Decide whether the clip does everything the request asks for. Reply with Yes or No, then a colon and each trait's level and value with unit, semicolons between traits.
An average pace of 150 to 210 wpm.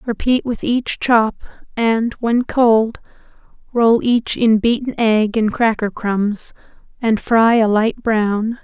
No: average, 140 wpm